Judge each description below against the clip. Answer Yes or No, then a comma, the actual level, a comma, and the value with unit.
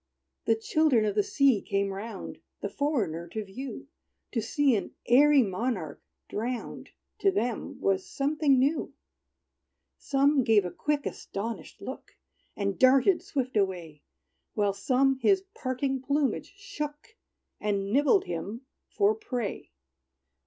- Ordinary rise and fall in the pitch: No, wide, 5.9 semitones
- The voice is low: No, very high, 255 Hz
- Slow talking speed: Yes, slow, 125 wpm